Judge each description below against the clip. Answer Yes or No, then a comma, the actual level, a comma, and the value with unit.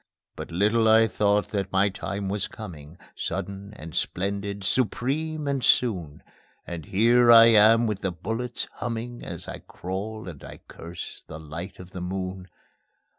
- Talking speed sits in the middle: Yes, average, 155 wpm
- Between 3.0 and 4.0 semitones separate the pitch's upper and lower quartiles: Yes, average, 3.7 semitones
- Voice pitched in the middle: No, low, 100 Hz